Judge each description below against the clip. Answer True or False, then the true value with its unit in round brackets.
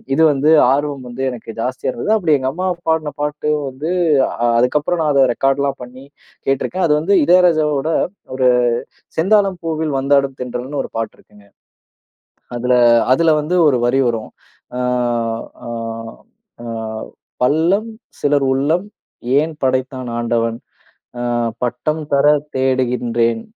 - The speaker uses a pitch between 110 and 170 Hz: True (140 Hz)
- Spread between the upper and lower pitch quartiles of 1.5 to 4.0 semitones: True (3.6 semitones)